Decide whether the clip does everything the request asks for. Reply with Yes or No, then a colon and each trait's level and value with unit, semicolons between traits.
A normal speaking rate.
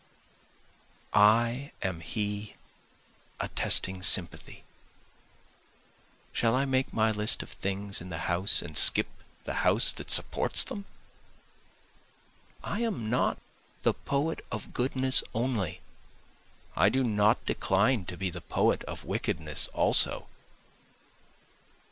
No: slow, 110 wpm